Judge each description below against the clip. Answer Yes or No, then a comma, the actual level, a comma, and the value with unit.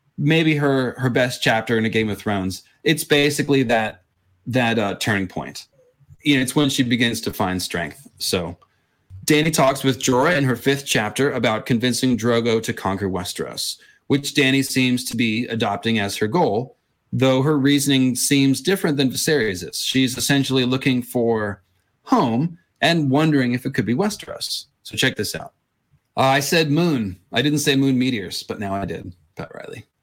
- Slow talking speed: No, average, 175 wpm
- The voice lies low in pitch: Yes, low, 130 Hz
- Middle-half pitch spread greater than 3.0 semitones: Yes, average, 3.7 semitones